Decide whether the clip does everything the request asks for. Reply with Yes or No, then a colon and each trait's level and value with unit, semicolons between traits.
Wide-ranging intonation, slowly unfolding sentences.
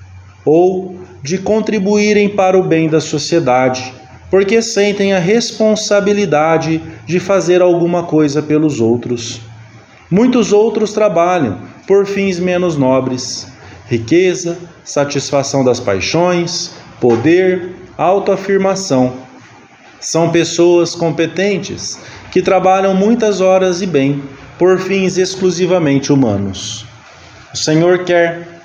Yes: wide, 5.7 semitones; slow, 100 wpm